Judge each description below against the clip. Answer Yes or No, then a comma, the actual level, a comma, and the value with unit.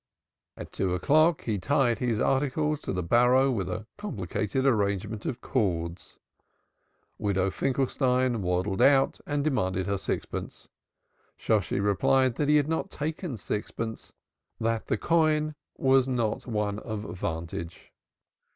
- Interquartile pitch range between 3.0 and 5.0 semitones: No, wide, 5.5 semitones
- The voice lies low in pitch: Yes, low, 115 Hz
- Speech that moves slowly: Yes, slow, 130 wpm